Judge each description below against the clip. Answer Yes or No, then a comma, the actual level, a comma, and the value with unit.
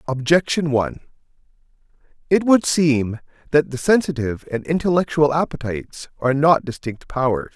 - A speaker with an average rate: No, slow, 120 wpm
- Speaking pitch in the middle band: Yes, medium, 145 Hz